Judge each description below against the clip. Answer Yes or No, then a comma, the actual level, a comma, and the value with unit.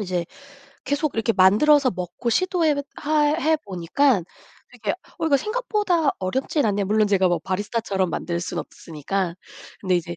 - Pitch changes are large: Yes, wide, 8.2 semitones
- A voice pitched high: Yes, high, 215 Hz